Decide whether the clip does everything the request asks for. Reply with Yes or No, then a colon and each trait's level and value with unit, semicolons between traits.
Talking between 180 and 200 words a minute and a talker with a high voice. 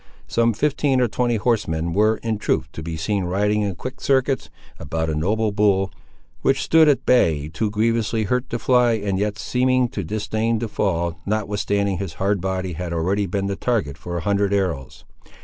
No: average, 185 wpm; low, 100 Hz